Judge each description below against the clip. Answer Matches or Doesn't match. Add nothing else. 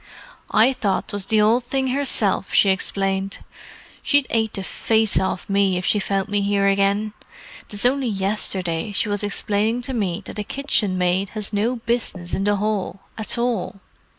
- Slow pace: Doesn't match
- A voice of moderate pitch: Doesn't match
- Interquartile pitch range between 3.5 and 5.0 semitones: Doesn't match